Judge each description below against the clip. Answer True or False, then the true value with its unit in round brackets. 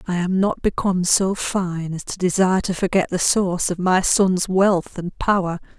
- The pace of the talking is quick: False (195 wpm)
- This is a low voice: False (185 Hz)